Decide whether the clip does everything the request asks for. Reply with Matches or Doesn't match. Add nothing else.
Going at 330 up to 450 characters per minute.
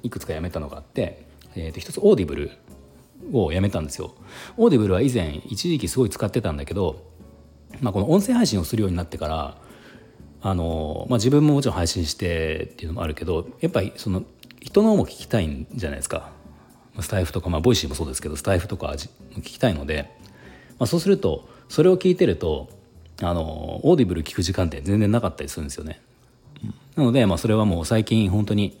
Matches